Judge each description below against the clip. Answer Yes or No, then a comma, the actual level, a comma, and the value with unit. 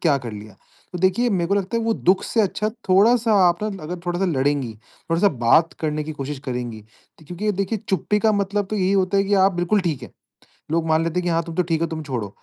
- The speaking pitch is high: No, medium, 175 Hz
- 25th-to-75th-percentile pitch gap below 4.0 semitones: No, average, 4.6 semitones